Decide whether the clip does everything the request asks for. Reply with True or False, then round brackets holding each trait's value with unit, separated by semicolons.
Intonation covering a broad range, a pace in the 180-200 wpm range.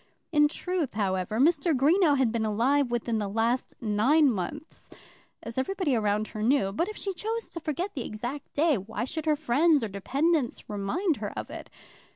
True (6.4 semitones; 185 wpm)